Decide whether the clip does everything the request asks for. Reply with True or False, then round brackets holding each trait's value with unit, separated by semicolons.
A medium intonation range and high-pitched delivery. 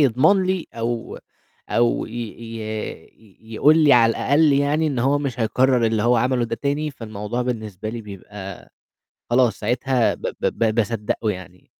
False (3.6 semitones; 120 Hz)